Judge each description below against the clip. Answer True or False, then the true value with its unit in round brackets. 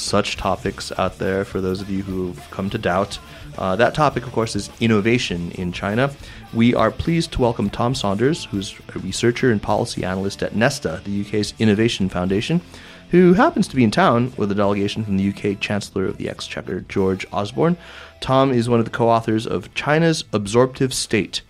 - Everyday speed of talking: True (195 wpm)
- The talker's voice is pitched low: True (110 Hz)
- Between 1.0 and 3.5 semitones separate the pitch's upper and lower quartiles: False (4.0 semitones)